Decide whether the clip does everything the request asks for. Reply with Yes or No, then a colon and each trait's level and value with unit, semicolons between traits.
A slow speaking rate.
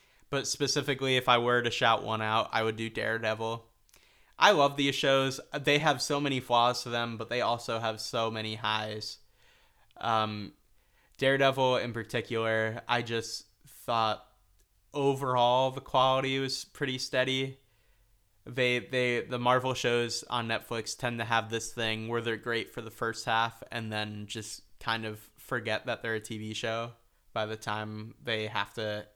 No: average, 165 wpm